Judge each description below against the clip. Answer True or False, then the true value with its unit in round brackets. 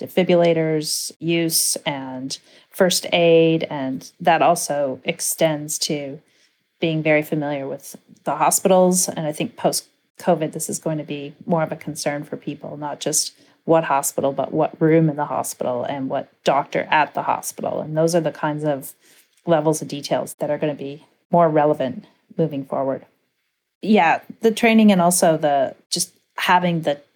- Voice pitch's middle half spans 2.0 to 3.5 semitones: True (2.8 semitones)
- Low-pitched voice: False (160 Hz)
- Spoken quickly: False (165 wpm)